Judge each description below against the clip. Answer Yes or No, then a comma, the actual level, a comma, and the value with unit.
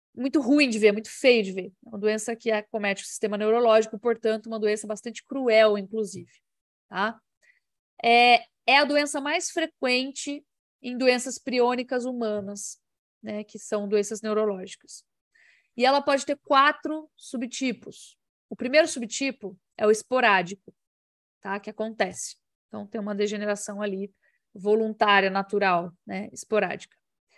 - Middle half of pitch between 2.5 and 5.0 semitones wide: Yes, average, 3.6 semitones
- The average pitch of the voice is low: No, high, 220 Hz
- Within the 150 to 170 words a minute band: No, average, 135 wpm